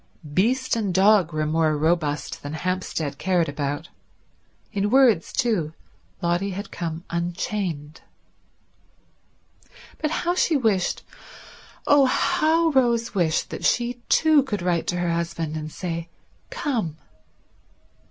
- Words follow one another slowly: Yes, slow, 120 wpm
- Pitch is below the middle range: No, medium, 180 Hz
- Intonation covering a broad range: Yes, wide, 6.5 semitones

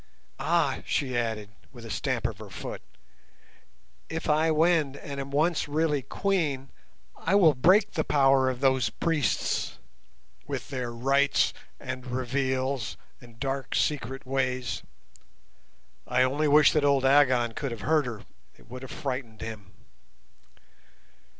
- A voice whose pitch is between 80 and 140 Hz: Yes, low, 135 Hz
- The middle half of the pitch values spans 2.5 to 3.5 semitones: Yes, average, 2.8 semitones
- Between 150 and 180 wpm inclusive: No, slow, 135 wpm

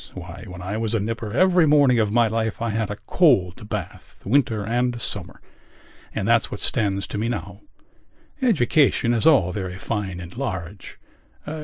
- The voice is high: No, low, 110 Hz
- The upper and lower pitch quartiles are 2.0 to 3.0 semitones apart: No, average, 3.4 semitones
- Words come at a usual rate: Yes, average, 170 wpm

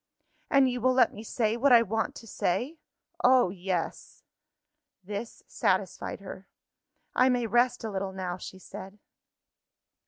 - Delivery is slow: No, average, 145 wpm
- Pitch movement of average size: Yes, average, 4.6 semitones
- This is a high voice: Yes, high, 225 Hz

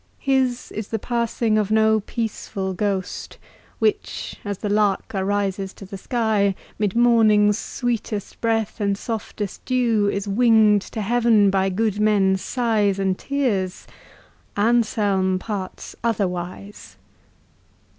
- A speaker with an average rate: No, slow, 120 wpm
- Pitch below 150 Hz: No, high, 210 Hz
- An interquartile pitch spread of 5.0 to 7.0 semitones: No, narrow, 2.6 semitones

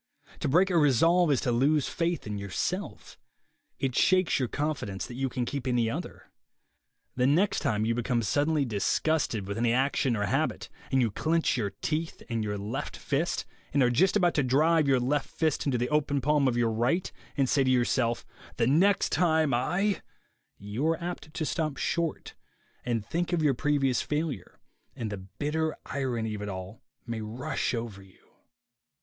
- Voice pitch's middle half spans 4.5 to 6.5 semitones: Yes, average, 5.1 semitones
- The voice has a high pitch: No, low, 135 Hz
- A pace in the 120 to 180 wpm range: No, average, 190 wpm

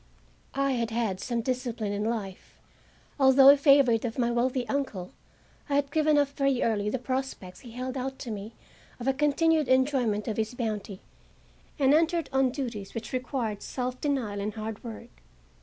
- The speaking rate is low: No, average, 175 wpm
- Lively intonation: No, average, 3.8 semitones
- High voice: Yes, very high, 250 Hz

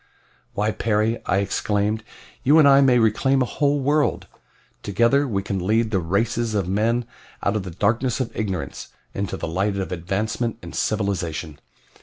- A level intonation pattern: No, average, 3.5 semitones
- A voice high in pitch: No, low, 110 Hz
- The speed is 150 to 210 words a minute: Yes, average, 165 wpm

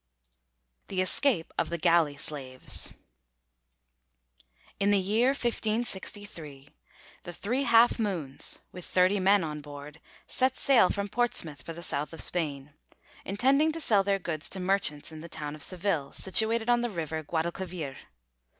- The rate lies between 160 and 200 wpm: No, average, 145 wpm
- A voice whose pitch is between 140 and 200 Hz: Yes, medium, 185 Hz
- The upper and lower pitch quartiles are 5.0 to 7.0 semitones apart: Yes, wide, 5.6 semitones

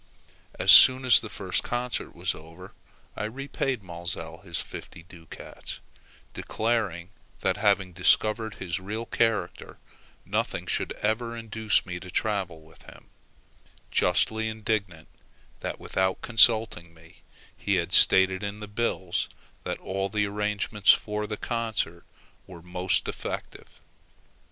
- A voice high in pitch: No, low, 100 Hz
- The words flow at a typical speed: No, slow, 125 wpm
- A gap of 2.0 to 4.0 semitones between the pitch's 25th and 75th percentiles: Yes, average, 3.6 semitones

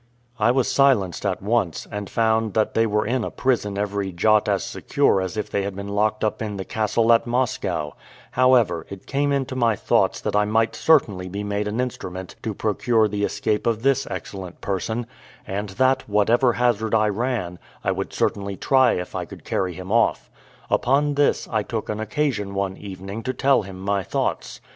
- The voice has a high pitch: No, low, 105 Hz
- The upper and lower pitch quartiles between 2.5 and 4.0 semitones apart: Yes, average, 3.4 semitones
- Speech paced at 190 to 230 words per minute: Yes, average, 195 wpm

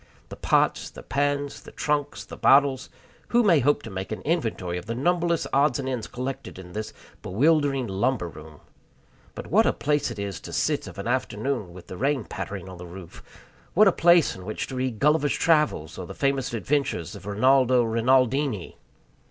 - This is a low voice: Yes, low, 130 Hz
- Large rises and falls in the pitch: Yes, wide, 6.1 semitones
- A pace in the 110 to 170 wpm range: No, average, 190 wpm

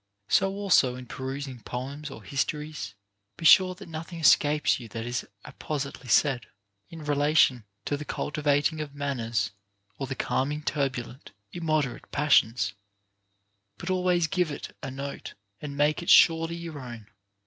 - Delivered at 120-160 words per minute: Yes, average, 150 wpm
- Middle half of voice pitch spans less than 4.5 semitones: Yes, average, 3.4 semitones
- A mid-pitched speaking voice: Yes, medium, 145 Hz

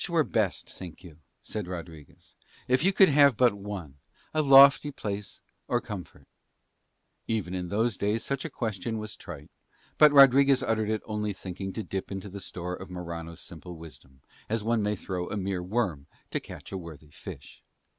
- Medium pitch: No, low, 100 Hz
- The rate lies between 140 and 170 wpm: No, average, 180 wpm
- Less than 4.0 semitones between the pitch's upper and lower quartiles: No, average, 4.9 semitones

